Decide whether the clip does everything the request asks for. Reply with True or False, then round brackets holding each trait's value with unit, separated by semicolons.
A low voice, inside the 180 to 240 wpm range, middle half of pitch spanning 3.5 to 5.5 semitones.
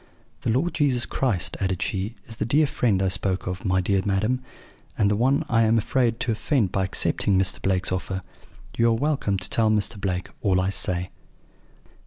True (105 Hz; 195 wpm; 4.0 semitones)